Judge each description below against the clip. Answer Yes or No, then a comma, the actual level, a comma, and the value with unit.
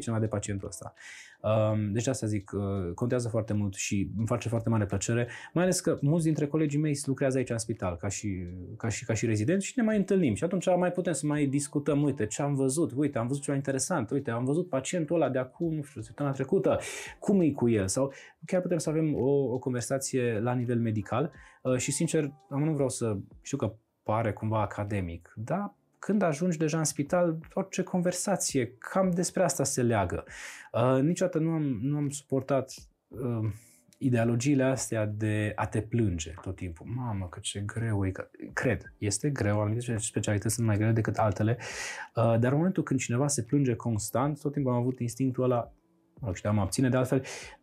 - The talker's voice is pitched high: No, low, 125 Hz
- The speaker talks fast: Yes, fast, 195 wpm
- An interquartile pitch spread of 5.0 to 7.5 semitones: Yes, average, 5.3 semitones